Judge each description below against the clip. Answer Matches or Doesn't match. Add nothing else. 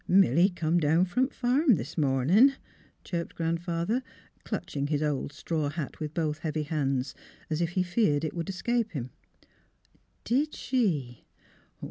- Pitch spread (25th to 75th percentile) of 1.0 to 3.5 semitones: Doesn't match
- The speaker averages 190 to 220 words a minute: Doesn't match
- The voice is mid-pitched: Matches